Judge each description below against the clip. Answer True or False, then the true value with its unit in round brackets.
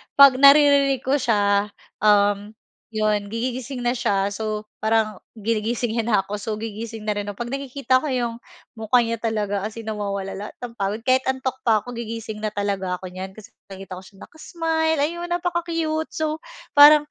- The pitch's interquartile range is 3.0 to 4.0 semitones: False (4.4 semitones)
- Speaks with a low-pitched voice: False (225 Hz)